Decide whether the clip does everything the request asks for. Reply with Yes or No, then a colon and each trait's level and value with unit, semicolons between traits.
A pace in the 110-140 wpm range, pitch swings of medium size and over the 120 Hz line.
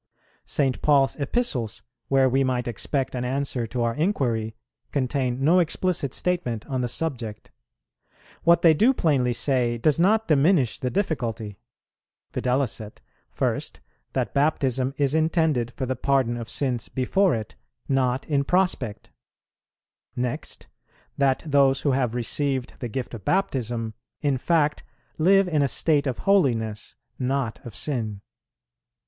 Yes: slow, 135 wpm; average, 3.9 semitones; low, 135 Hz